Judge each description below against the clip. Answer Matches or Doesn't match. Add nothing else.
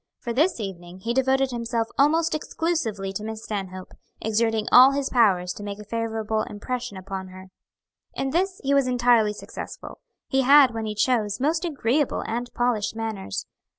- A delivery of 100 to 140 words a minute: Doesn't match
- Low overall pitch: Doesn't match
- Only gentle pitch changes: Doesn't match